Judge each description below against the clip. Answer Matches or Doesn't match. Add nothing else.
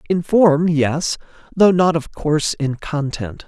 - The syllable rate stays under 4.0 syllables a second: Matches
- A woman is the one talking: Doesn't match